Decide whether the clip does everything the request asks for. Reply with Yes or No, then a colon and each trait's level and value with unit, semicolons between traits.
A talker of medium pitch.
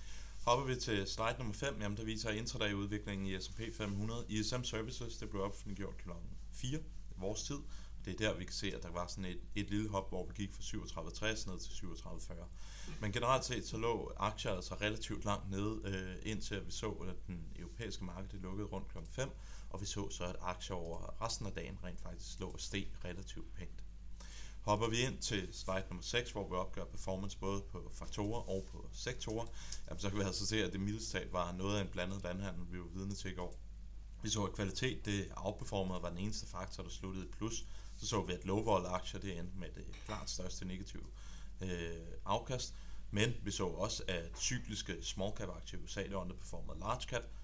No: very low, 95 Hz